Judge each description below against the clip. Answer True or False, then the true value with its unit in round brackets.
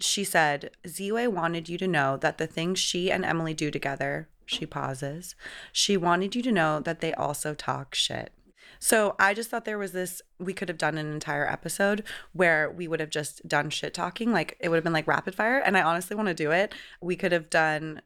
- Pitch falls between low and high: True (170 Hz)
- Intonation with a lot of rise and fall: False (4.2 semitones)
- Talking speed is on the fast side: True (225 wpm)